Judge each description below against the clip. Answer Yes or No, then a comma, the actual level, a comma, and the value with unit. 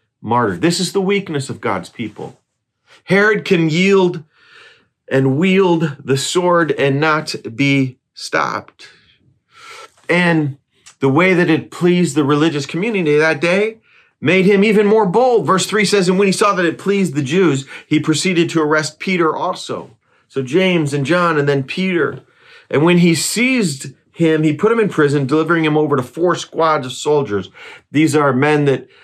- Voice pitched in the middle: Yes, medium, 165 Hz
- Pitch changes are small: No, average, 4.3 semitones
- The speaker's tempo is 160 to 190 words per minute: Yes, average, 170 wpm